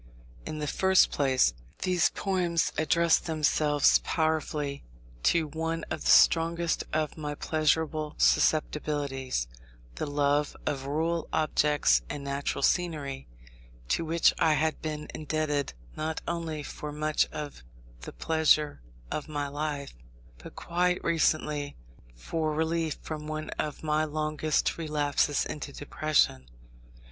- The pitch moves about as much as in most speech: No, narrow, 1.7 semitones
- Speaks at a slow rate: Yes, slow, 120 wpm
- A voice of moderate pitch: Yes, medium, 155 Hz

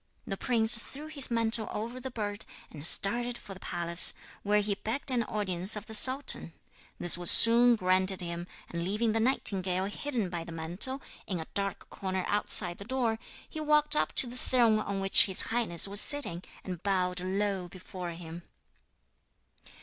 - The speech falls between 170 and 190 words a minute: Yes, average, 175 wpm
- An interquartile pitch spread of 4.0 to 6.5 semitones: Yes, average, 4.5 semitones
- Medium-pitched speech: No, high, 205 Hz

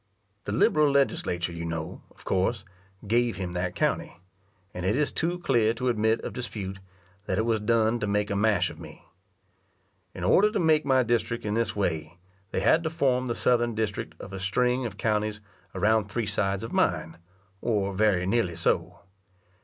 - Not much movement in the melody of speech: No, average, 3.7 semitones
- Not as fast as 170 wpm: No, average, 185 wpm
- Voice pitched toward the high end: No, low, 110 Hz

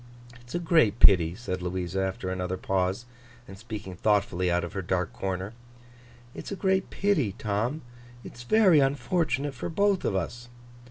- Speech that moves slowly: No, average, 160 wpm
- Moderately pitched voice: No, low, 105 Hz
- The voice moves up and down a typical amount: No, wide, 7.2 semitones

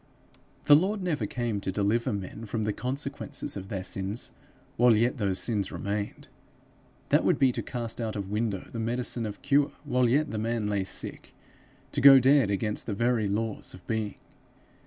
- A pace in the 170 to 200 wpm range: Yes, average, 180 wpm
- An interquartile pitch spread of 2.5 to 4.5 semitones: Yes, average, 3.5 semitones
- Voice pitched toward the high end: No, low, 115 Hz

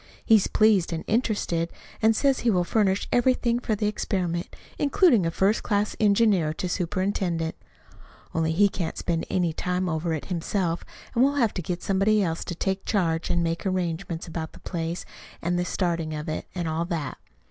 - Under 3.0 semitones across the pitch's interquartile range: No, average, 3.8 semitones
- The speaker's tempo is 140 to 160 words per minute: No, average, 180 wpm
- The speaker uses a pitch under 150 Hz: No, medium, 180 Hz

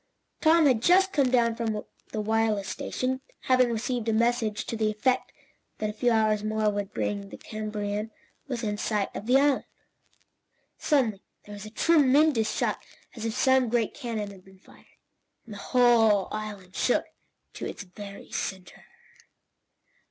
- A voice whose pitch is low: No, high, 220 Hz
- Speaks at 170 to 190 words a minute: No, average, 160 wpm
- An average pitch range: Yes, average, 3.1 semitones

